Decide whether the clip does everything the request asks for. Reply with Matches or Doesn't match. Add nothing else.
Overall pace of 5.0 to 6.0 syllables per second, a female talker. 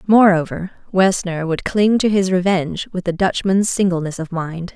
Doesn't match